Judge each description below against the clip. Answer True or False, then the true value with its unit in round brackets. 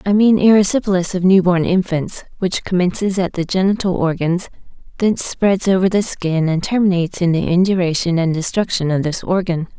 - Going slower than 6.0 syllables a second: True (5.5 syllables/s)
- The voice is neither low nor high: True (180 Hz)